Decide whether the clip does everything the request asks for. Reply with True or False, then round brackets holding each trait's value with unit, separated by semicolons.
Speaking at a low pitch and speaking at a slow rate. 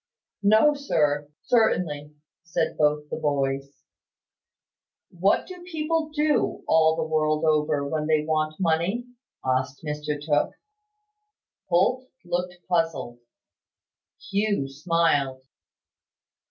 False (160 Hz; 100 wpm)